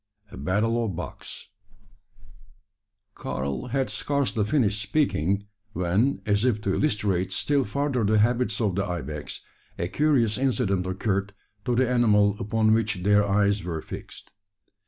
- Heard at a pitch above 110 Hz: No, low, 105 Hz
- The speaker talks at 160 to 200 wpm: No, slow, 135 wpm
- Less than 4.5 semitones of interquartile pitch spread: Yes, average, 3.8 semitones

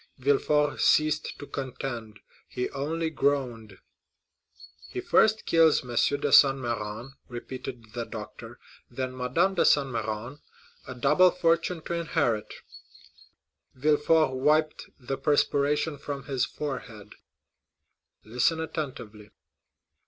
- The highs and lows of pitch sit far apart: No, average, 4.2 semitones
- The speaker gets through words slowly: Yes, slow, 105 wpm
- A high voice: No, low, 135 Hz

